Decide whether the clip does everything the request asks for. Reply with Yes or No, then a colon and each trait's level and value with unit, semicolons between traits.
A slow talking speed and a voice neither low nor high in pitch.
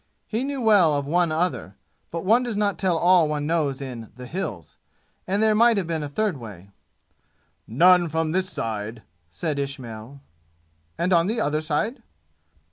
No: average, 170 wpm; medium, 160 Hz